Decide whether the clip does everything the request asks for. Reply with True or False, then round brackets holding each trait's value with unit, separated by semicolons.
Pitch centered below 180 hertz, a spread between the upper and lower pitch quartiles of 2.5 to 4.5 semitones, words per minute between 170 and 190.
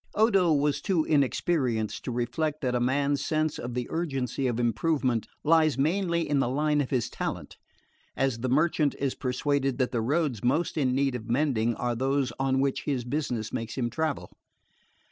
True (135 Hz; 3.7 semitones; 180 wpm)